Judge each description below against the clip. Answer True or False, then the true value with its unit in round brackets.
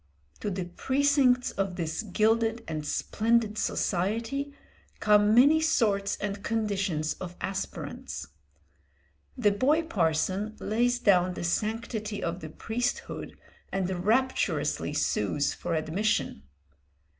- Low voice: False (210 Hz)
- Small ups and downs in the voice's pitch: False (4.3 semitones)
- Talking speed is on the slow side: True (110 wpm)